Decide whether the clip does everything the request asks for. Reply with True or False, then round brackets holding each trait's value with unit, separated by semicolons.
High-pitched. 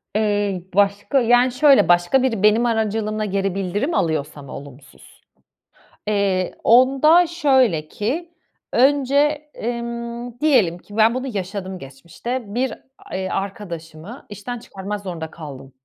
True (210 Hz)